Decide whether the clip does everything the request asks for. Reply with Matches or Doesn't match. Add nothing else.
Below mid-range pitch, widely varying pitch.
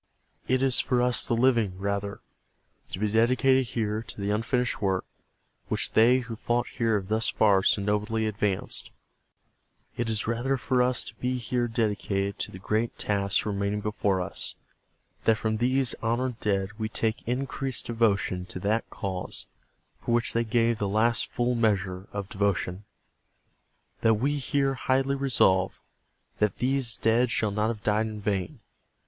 Doesn't match